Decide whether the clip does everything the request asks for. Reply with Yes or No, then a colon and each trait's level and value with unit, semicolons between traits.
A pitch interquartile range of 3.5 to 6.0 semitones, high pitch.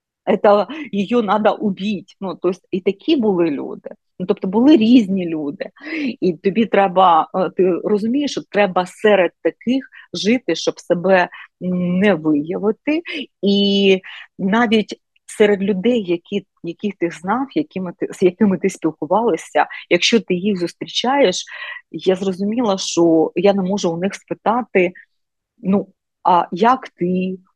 No: average, 3.1 semitones; high, 195 Hz